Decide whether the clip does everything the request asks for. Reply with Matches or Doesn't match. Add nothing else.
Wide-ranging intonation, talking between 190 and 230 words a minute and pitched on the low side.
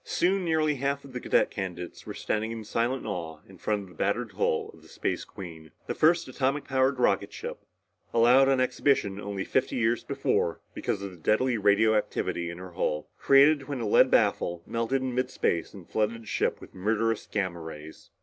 Matches